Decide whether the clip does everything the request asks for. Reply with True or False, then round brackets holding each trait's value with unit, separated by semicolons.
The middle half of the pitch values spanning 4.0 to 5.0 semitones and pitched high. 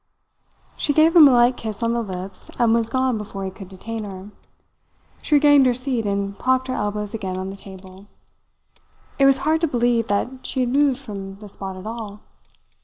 True (4.6 semitones; 225 Hz)